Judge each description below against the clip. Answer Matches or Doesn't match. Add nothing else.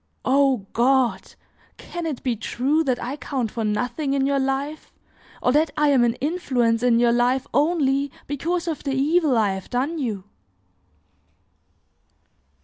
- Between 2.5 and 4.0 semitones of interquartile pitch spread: Matches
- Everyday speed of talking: Matches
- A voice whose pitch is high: Matches